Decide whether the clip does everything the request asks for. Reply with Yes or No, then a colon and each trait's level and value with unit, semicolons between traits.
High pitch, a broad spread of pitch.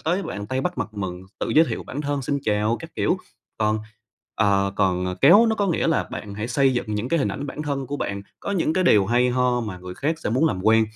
No: low, 125 Hz; wide, 6.4 semitones